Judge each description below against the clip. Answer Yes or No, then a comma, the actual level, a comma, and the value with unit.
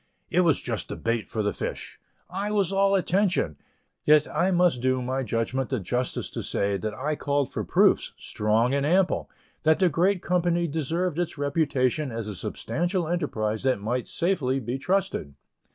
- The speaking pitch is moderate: Yes, medium, 145 Hz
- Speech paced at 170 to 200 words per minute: Yes, average, 175 wpm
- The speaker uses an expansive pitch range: Yes, wide, 6.4 semitones